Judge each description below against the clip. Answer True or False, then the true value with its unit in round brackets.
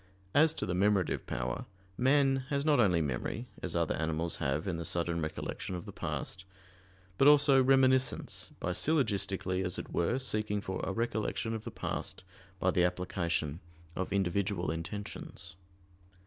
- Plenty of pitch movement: True (6.2 semitones)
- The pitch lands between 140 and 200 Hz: False (95 Hz)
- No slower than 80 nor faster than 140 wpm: False (155 wpm)